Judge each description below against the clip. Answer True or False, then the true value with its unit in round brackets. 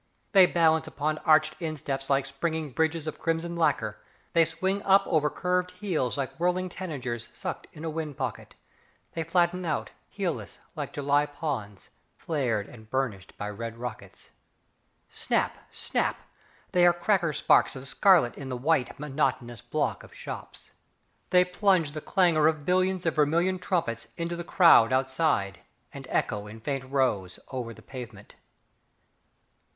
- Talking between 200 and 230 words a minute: False (150 wpm)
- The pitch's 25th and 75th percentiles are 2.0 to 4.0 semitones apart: False (4.8 semitones)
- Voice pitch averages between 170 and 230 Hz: False (155 Hz)